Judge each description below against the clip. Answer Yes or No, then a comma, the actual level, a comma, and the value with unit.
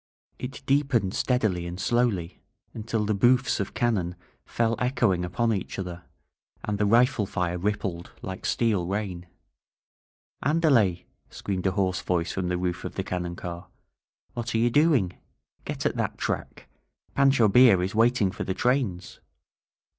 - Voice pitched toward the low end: Yes, low, 100 Hz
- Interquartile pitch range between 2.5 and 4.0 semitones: No, average, 5.1 semitones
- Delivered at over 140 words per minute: Yes, average, 150 wpm